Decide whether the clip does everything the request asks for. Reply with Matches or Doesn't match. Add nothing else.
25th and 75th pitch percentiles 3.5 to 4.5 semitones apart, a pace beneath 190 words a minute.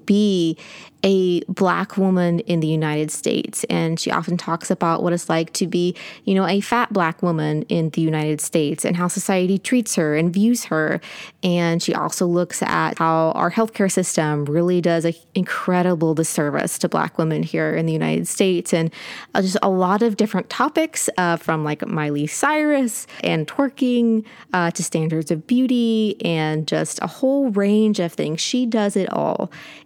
Matches